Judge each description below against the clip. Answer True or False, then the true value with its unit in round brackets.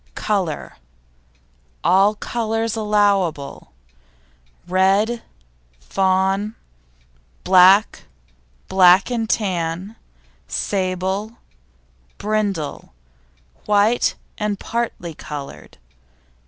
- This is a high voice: True (195 Hz)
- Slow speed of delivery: True (60 wpm)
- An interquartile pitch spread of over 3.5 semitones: False (2.7 semitones)